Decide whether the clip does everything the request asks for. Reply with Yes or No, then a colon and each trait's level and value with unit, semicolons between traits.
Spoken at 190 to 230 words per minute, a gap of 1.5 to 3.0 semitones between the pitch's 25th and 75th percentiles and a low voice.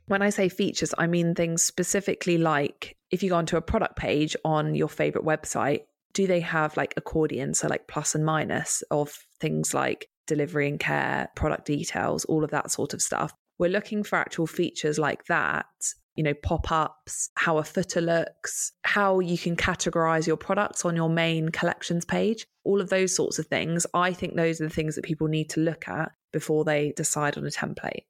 No: average, 200 wpm; narrow, 2.5 semitones; medium, 165 Hz